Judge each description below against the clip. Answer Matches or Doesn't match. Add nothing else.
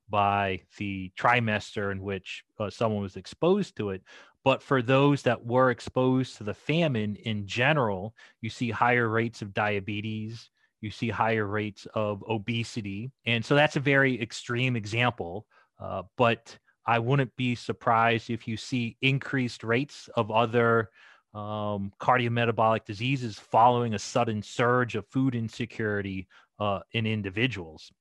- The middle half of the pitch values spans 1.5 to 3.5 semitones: Matches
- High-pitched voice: Doesn't match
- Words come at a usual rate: Matches